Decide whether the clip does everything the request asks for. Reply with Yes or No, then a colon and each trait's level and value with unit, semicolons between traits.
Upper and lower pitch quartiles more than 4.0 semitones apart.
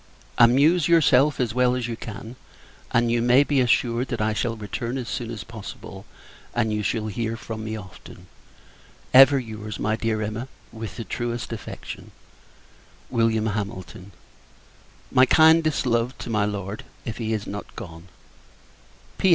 No: narrow, 2.6 semitones